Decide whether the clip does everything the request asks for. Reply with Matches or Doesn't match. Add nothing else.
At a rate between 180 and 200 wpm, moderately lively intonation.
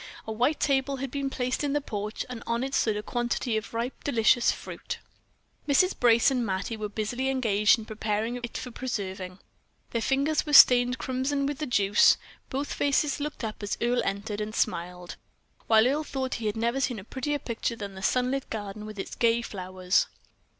Matches